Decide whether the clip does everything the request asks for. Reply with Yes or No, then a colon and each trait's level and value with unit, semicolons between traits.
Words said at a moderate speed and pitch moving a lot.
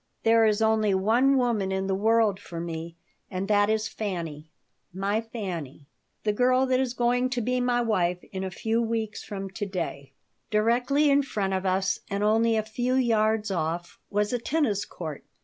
No: average, 185 wpm; average, 3.6 semitones